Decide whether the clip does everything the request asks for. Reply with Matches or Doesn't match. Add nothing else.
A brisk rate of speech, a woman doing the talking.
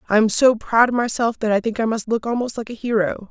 Matches